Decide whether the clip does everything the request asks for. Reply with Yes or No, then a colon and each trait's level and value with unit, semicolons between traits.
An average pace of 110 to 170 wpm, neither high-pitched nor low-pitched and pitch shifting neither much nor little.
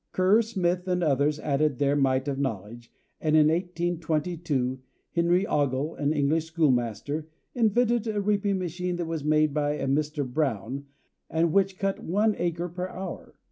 Yes: average, 160 wpm; medium, 160 Hz; average, 4.1 semitones